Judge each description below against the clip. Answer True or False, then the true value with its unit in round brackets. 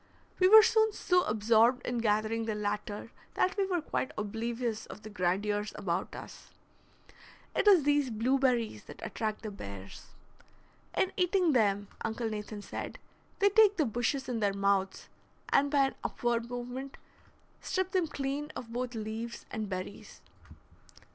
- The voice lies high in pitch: True (235 Hz)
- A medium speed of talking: True (150 wpm)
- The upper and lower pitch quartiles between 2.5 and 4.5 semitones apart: False (5.2 semitones)